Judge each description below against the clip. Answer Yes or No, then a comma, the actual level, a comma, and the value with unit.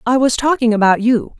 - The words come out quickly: Yes, fast, 215 wpm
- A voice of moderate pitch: No, high, 240 Hz